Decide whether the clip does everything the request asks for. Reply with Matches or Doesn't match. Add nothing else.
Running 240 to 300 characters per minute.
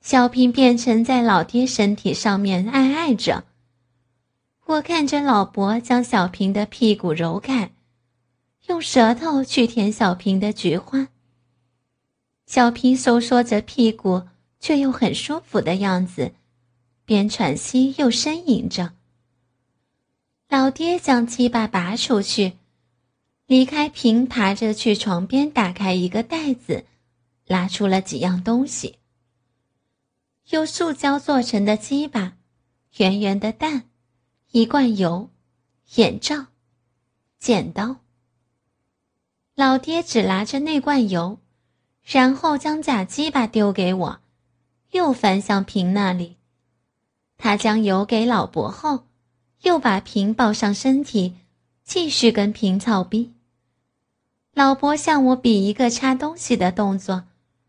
Doesn't match